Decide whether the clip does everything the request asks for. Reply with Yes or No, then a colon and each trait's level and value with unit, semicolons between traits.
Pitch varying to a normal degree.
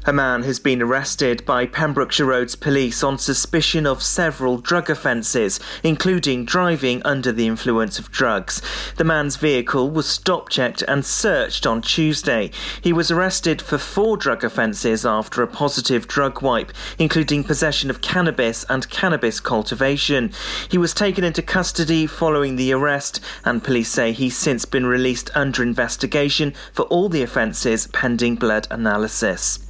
Yes: average, 4.1 semitones